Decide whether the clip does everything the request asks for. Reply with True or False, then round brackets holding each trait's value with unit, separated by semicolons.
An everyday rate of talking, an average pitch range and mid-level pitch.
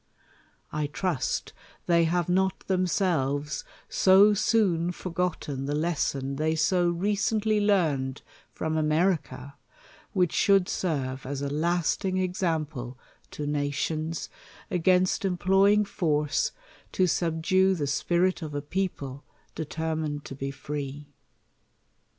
False (105 wpm; 4.1 semitones; 165 Hz)